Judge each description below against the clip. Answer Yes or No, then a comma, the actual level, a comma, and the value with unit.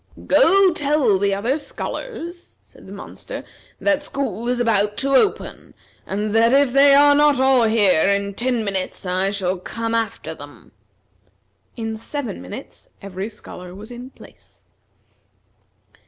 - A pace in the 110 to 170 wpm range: Yes, average, 140 wpm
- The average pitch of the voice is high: Yes, high, 230 Hz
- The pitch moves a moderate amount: No, wide, 5.8 semitones